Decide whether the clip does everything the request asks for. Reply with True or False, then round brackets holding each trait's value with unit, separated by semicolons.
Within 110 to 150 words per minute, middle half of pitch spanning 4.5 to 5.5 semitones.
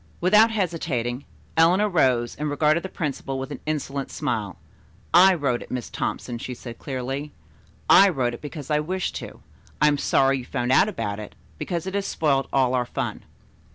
False (185 wpm; 5.1 semitones)